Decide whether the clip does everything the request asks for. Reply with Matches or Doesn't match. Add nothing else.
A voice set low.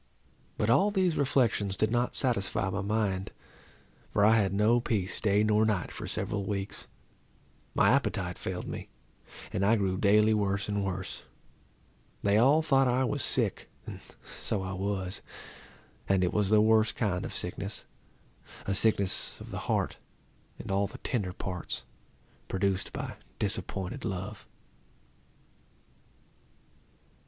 Matches